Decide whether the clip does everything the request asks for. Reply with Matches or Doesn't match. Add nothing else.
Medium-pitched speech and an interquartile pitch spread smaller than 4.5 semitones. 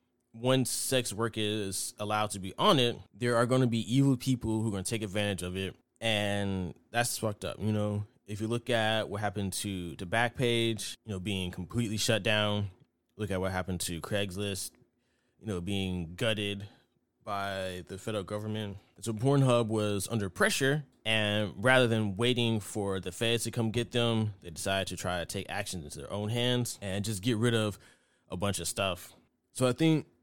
Doesn't match